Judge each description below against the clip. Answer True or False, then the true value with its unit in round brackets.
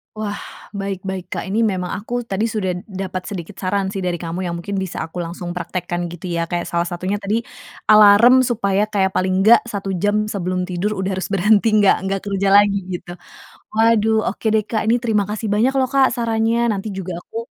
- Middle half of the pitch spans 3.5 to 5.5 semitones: False (2.9 semitones)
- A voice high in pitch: True (200 Hz)